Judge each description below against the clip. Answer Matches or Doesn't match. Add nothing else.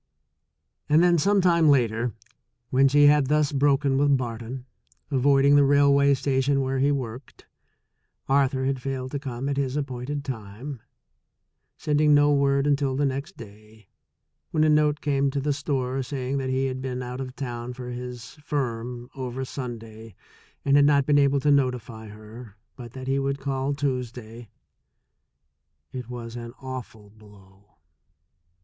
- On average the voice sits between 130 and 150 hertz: Matches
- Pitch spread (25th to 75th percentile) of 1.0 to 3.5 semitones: Matches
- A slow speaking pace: Doesn't match